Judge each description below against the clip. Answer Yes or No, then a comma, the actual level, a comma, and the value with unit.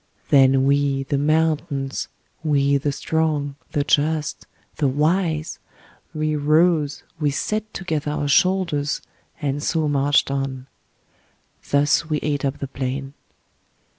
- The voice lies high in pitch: No, medium, 145 Hz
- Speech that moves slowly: Yes, slow, 120 wpm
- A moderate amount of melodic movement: No, narrow, 2.0 semitones